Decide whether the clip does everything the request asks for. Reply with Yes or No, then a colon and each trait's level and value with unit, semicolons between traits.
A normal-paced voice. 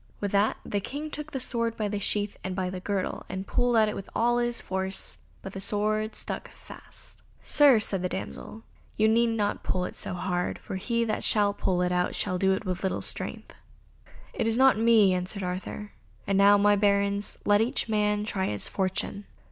No: fast, 210 wpm